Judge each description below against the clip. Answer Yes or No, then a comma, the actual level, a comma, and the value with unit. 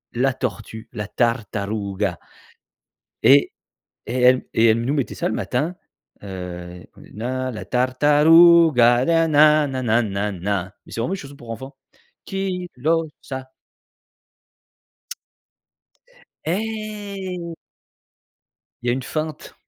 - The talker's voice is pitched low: Yes, low, 130 Hz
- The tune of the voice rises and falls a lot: Yes, wide, 6.3 semitones